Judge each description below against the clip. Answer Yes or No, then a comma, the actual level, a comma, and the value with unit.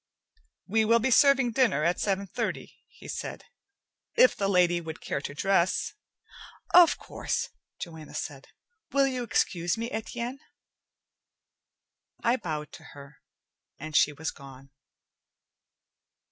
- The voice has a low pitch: No, high, 190 Hz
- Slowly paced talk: Yes, slow, 130 wpm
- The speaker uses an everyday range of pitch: No, wide, 7.5 semitones